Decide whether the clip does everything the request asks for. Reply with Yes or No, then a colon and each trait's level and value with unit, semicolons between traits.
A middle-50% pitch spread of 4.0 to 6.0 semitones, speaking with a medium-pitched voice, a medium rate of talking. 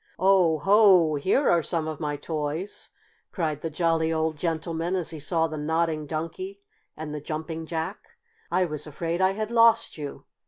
No: average, 2.7 semitones; medium, 160 Hz; average, 170 wpm